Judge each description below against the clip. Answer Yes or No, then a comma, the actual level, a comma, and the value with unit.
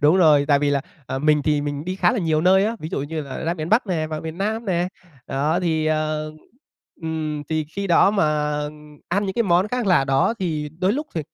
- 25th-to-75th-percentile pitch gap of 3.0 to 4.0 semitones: Yes, average, 3.7 semitones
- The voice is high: No, medium, 160 Hz